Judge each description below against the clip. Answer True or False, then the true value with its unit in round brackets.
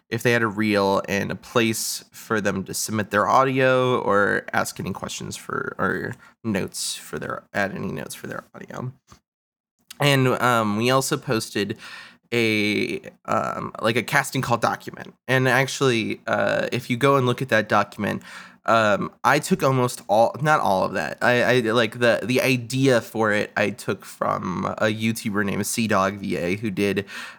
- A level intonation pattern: False (3.5 semitones)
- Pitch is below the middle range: True (120 Hz)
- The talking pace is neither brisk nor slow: True (175 wpm)